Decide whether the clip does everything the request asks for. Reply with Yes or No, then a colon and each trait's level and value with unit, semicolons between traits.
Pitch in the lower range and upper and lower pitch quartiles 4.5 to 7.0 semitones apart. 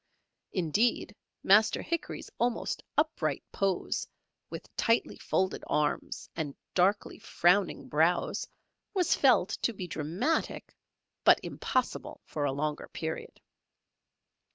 No: medium, 185 Hz; average, 5.2 semitones